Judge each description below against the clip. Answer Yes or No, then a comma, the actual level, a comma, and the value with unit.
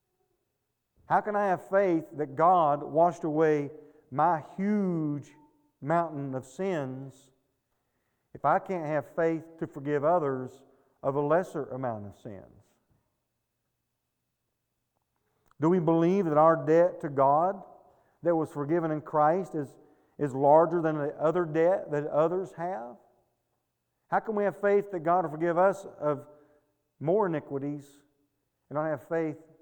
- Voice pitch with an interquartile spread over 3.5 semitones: No, average, 3.1 semitones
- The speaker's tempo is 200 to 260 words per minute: No, average, 140 wpm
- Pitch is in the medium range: Yes, medium, 155 Hz